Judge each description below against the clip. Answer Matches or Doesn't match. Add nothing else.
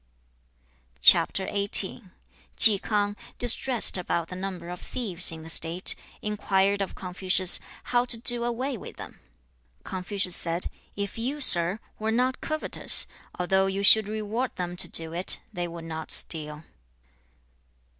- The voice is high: Matches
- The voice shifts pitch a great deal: Doesn't match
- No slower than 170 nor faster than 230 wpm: Doesn't match